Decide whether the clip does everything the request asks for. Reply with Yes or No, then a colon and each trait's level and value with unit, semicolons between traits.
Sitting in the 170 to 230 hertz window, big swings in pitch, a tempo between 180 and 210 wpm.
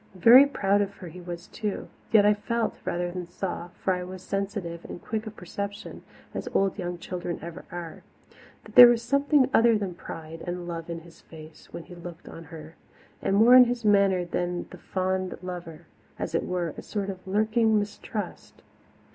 No: medium, 185 Hz; average, 3.3 semitones; average, 190 wpm